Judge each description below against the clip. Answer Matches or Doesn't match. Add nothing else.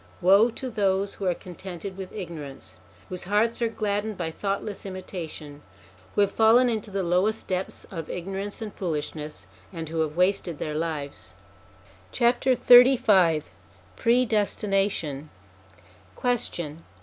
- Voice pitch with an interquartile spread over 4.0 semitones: Matches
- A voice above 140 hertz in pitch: Matches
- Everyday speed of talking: Doesn't match